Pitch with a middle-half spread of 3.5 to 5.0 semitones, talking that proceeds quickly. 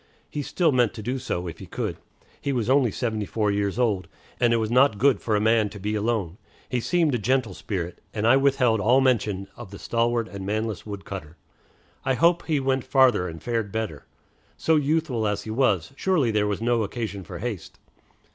Yes: average, 4.1 semitones; fast, 210 wpm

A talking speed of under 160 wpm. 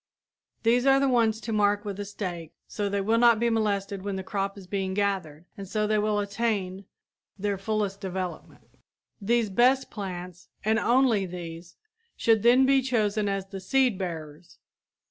No: average, 170 wpm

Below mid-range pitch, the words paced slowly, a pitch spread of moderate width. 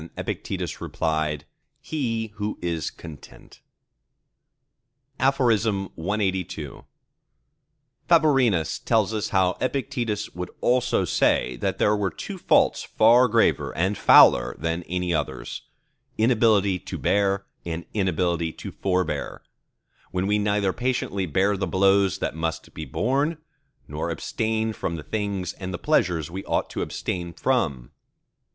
Yes: very low, 95 Hz; slow, 120 wpm; average, 4.5 semitones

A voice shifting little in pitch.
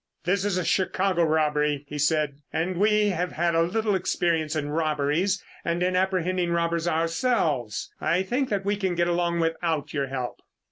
No: average, 3.2 semitones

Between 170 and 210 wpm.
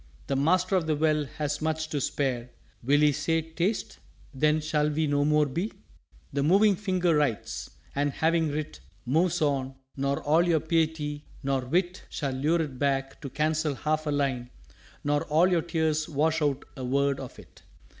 Yes: average, 175 wpm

